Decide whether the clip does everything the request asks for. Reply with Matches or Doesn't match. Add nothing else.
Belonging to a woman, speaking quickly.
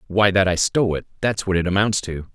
Doesn't match